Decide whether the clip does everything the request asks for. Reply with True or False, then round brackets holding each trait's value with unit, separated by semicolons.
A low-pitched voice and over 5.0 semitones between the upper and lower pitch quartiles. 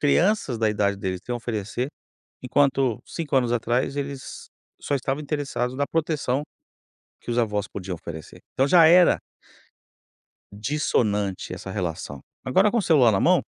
True (125 Hz; 5.6 semitones)